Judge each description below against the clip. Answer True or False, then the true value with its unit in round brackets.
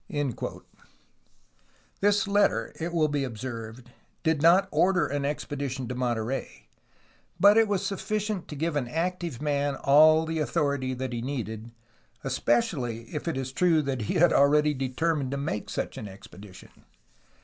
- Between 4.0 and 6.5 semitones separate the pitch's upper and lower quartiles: True (4.8 semitones)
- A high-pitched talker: False (145 Hz)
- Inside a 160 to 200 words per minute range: False (150 wpm)